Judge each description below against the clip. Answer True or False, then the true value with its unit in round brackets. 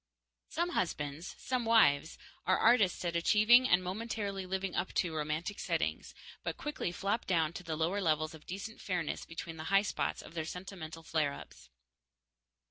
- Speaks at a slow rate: False (170 wpm)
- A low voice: False (180 Hz)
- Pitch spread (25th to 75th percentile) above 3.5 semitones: True (4.0 semitones)